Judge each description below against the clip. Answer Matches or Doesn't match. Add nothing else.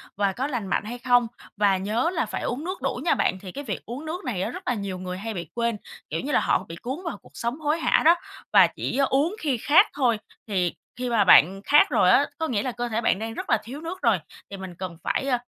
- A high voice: Matches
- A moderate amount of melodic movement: Doesn't match